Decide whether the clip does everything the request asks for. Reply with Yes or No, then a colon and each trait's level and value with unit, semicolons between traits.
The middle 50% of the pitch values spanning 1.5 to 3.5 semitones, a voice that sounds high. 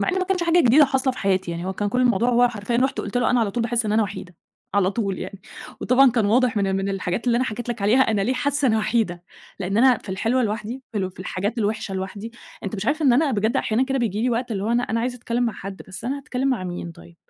No: average, 4.1 semitones; high, 230 Hz